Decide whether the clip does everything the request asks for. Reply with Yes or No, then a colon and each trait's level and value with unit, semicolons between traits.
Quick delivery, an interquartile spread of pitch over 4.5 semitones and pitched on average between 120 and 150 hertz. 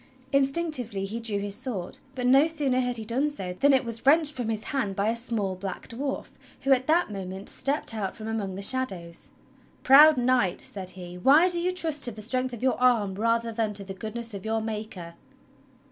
No: fast, 210 wpm; average, 5.0 semitones; high, 230 Hz